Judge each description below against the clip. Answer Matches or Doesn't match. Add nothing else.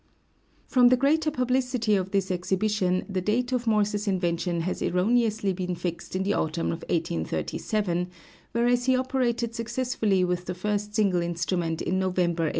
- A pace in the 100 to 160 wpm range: Matches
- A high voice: Matches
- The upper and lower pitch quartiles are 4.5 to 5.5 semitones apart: Matches